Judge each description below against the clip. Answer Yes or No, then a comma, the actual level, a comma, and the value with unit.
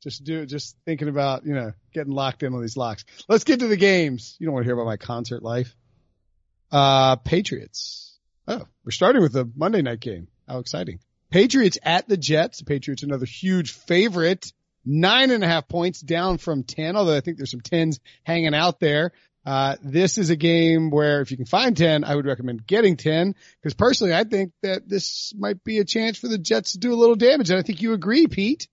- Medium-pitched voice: Yes, medium, 160 Hz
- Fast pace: Yes, fast, 220 wpm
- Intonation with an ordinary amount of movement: No, wide, 6.4 semitones